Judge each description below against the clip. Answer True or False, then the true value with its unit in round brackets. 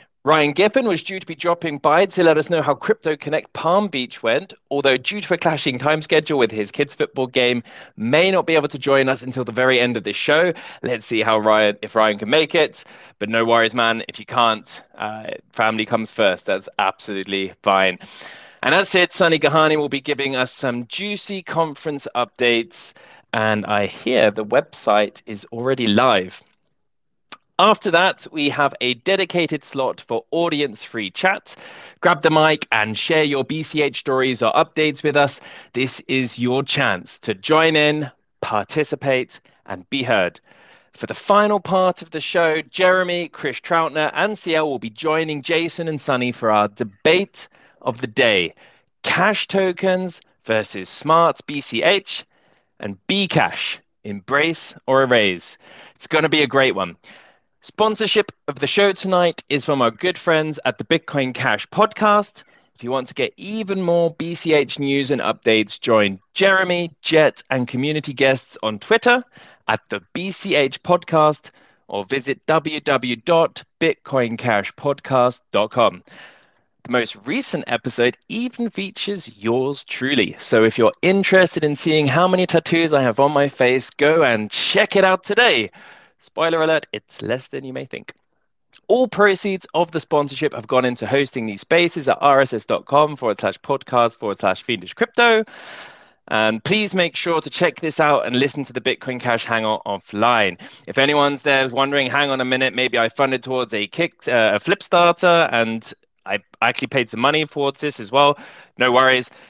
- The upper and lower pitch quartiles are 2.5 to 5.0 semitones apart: False (5.5 semitones)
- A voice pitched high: False (145 Hz)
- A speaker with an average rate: True (165 wpm)